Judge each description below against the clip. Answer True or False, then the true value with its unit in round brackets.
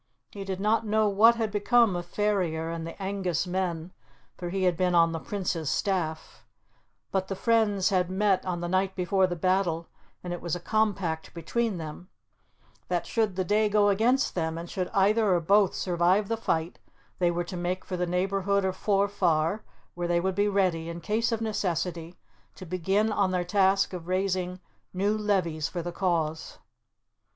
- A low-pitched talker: False (185 Hz)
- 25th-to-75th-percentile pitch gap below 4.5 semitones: True (2.8 semitones)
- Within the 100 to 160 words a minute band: False (185 wpm)